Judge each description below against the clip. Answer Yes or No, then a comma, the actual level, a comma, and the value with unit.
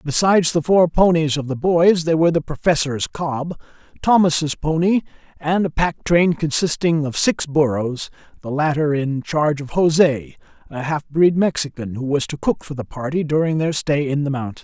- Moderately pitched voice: Yes, medium, 150 Hz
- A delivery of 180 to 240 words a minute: Yes, average, 185 wpm